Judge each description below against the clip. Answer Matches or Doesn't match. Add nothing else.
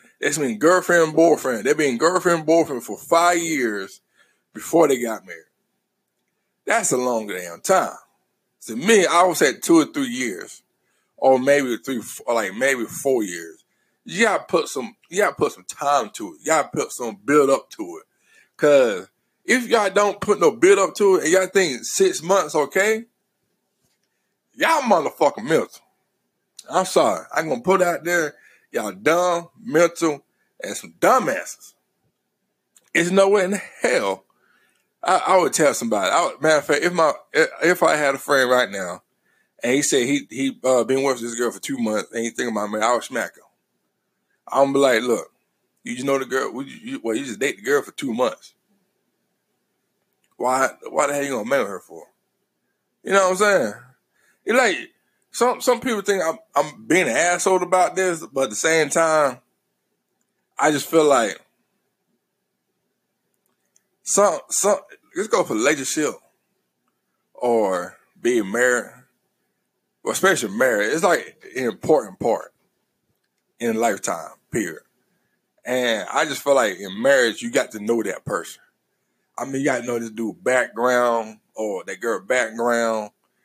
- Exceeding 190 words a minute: Doesn't match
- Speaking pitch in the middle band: Matches